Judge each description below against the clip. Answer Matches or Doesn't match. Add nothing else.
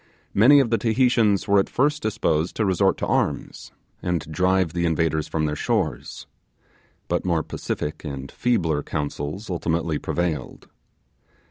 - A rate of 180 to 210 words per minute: Doesn't match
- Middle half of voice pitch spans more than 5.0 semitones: Matches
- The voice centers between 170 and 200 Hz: Doesn't match